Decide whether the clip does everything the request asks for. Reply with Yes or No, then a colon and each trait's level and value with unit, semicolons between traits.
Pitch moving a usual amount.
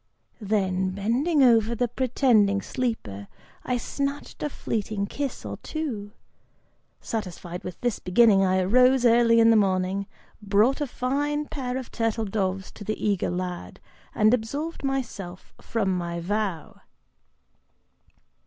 Yes: average, 4.7 semitones